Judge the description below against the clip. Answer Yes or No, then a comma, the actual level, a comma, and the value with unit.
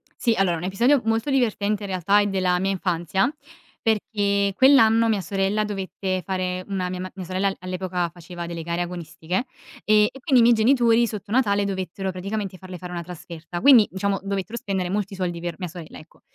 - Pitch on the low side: No, high, 195 Hz